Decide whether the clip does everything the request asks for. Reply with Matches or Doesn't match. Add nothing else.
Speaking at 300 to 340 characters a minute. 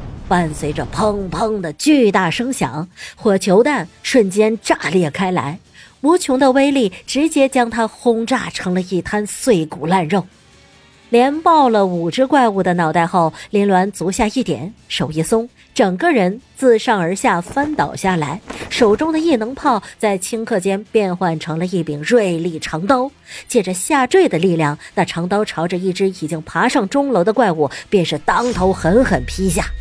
Doesn't match